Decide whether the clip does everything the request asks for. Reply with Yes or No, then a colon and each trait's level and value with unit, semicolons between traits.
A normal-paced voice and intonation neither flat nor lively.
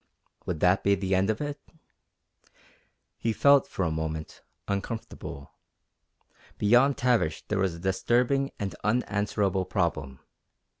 No: slow, 120 wpm; average, 4.8 semitones